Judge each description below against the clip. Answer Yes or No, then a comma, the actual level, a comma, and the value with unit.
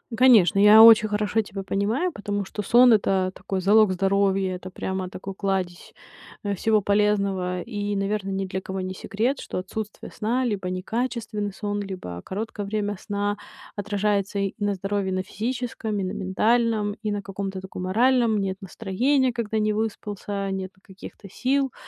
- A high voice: Yes, high, 205 Hz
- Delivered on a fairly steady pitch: Yes, narrow, 2.2 semitones